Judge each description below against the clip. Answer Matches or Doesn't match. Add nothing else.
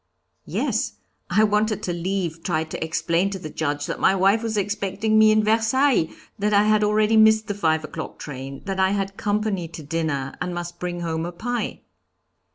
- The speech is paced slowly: Doesn't match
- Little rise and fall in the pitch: Doesn't match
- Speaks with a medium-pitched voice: Doesn't match